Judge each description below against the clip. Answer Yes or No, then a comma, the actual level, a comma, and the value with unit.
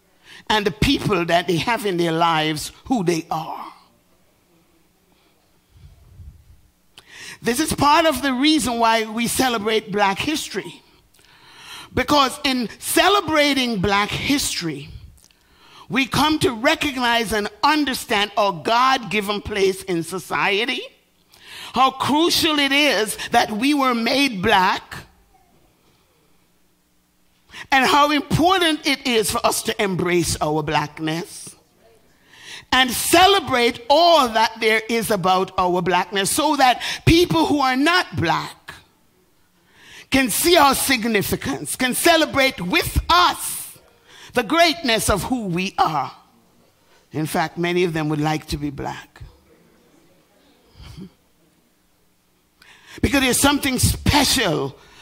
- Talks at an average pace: No, slow, 115 wpm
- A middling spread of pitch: No, wide, 7.8 semitones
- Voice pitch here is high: Yes, high, 230 Hz